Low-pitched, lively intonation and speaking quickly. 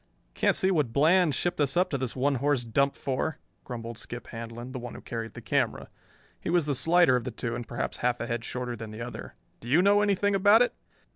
Yes: low, 130 Hz; wide, 6.3 semitones; fast, 235 wpm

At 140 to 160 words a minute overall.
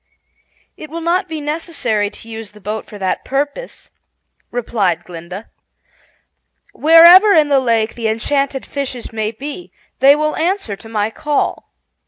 Yes: average, 145 wpm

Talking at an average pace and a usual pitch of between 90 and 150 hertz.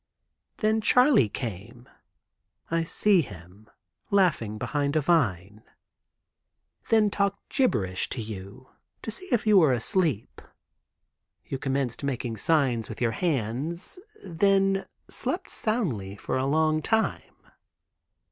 No: slow, 115 wpm; medium, 140 Hz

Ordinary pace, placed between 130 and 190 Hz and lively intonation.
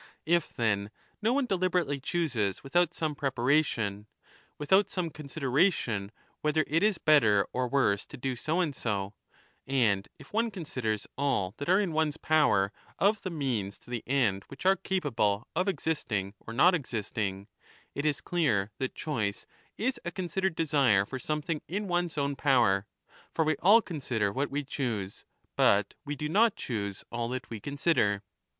Yes: average, 170 wpm; medium, 140 Hz; wide, 7.3 semitones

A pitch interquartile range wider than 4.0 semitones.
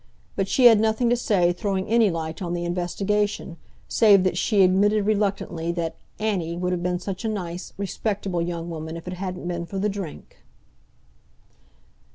No: average, 3.1 semitones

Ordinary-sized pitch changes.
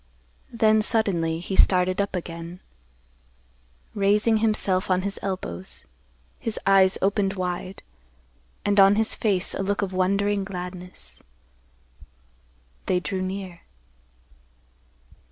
No: narrow, 1.9 semitones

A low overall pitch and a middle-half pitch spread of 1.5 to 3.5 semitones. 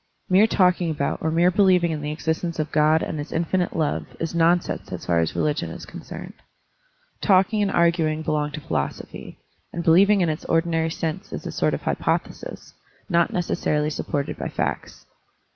No: medium, 165 Hz; narrow, 2.6 semitones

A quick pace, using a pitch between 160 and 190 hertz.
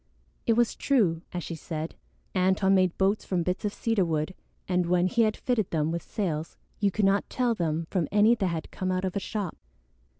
Yes: fast, 210 wpm; medium, 185 Hz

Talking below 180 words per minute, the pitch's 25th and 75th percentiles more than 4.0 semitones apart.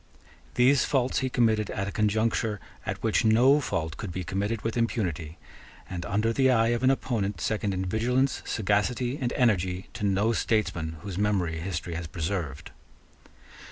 Yes: average, 160 wpm; average, 4.4 semitones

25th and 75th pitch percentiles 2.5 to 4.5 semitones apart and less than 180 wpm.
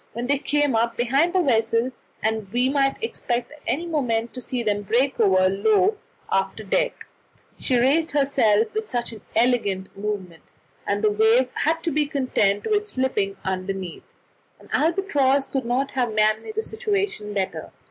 No: wide, 5.5 semitones; average, 170 wpm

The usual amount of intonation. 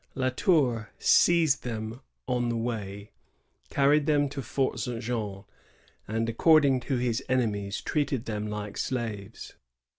Yes: average, 3.7 semitones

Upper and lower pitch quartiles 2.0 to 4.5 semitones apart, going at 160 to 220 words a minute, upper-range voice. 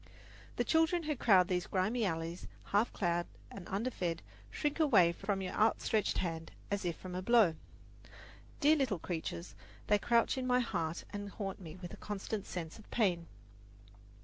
No: average, 5.1 semitones; average, 165 wpm; high, 195 Hz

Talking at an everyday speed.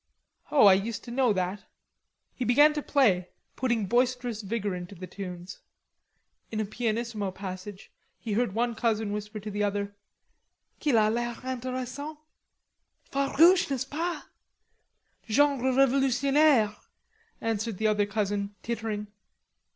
No: slow, 130 wpm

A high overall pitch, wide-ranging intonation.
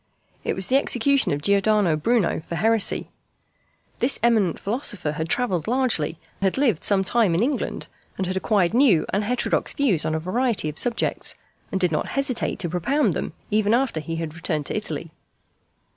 Yes: high, 200 Hz; wide, 6.4 semitones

